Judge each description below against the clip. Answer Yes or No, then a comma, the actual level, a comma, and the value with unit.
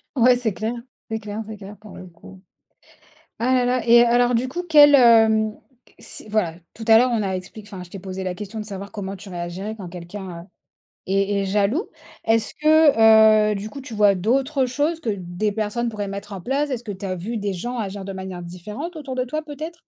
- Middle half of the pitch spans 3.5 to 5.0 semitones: Yes, average, 4.0 semitones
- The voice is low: No, high, 215 Hz